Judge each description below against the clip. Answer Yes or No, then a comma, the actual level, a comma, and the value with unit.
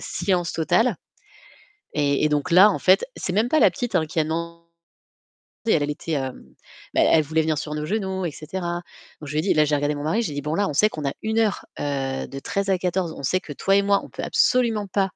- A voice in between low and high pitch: Yes, medium, 170 Hz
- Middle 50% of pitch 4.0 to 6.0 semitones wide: Yes, average, 4.7 semitones